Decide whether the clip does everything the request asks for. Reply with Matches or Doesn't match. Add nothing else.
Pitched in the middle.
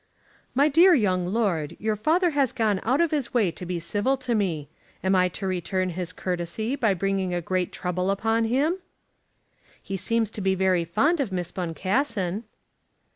Doesn't match